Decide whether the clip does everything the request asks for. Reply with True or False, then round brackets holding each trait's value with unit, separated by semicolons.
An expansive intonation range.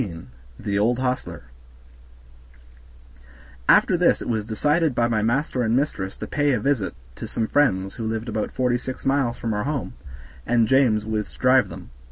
False (3.5 semitones)